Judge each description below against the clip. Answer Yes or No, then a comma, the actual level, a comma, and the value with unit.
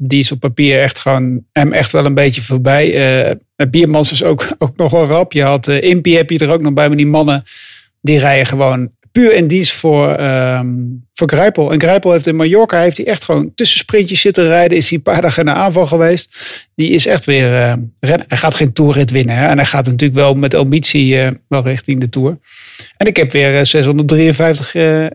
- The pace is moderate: No, fast, 220 wpm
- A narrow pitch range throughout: No, average, 3.4 semitones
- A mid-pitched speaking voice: Yes, medium, 145 Hz